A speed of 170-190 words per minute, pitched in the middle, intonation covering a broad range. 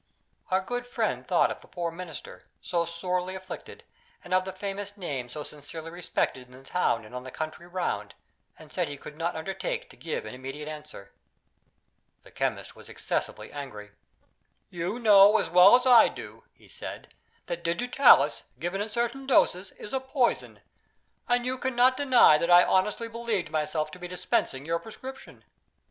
Yes: average, 175 wpm; medium, 180 Hz; wide, 6.8 semitones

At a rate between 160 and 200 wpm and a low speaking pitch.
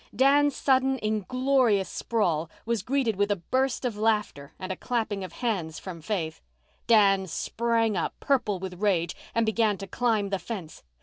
No: average, 165 wpm; high, 210 Hz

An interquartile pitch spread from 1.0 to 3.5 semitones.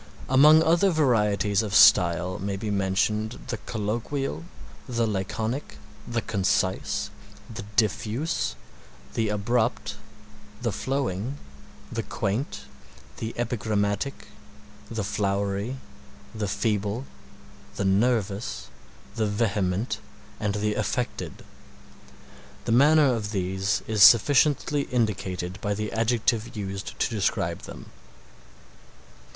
Yes: average, 3.2 semitones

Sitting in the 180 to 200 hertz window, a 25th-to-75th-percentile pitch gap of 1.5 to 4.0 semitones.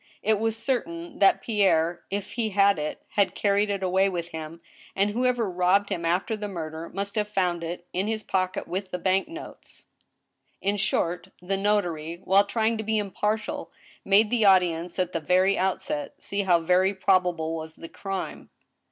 Yes: high, 190 Hz; average, 2.9 semitones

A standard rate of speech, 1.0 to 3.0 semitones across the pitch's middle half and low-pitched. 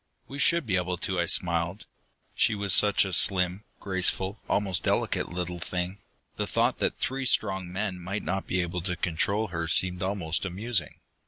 Yes: average, 175 wpm; narrow, 2.4 semitones; very low, 95 Hz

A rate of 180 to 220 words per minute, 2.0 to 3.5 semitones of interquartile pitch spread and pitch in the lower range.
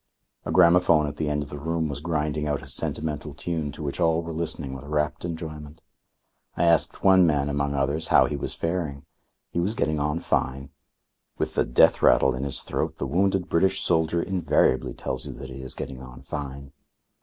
Yes: average, 200 wpm; average, 3.0 semitones; very low, 75 Hz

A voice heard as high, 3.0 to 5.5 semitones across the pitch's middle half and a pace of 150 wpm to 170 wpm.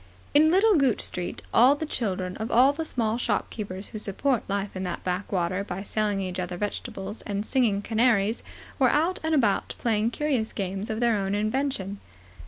No: high, 215 Hz; average, 4.7 semitones; average, 180 wpm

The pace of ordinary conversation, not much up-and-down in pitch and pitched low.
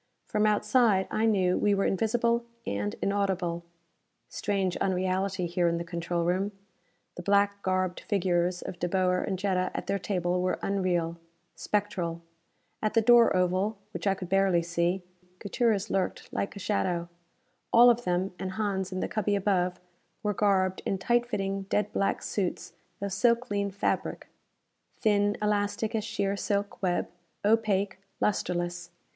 No: average, 150 wpm; narrow, 2.3 semitones; high, 195 Hz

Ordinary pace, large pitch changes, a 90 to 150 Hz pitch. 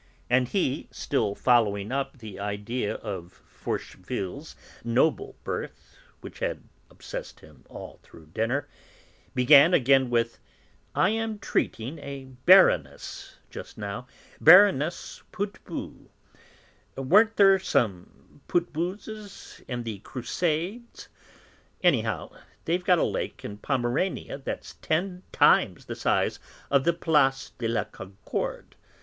No: slow, 115 wpm; wide, 7.6 semitones; low, 135 Hz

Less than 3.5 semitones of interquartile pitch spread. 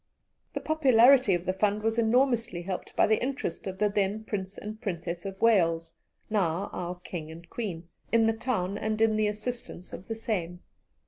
No: average, 3.9 semitones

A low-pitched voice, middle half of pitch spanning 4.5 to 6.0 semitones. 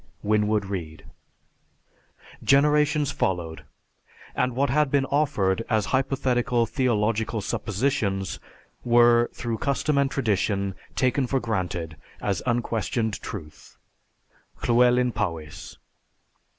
Yes: low, 115 Hz; average, 5.0 semitones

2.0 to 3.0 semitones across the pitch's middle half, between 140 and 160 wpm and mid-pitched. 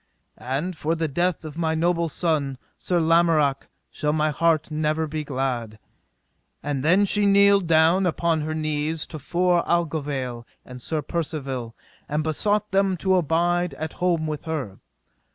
Yes: average, 2.7 semitones; average, 155 wpm; medium, 160 Hz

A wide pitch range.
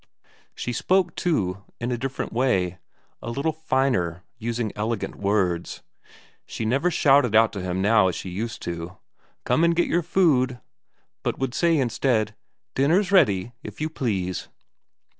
Yes: wide, 7.1 semitones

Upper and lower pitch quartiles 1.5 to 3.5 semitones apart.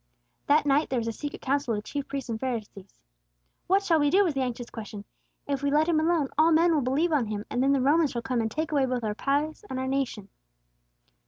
No: average, 4.4 semitones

